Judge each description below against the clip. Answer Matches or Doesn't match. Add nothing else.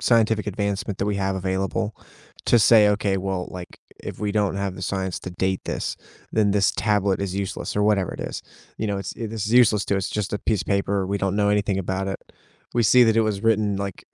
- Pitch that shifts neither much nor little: Doesn't match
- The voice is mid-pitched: Doesn't match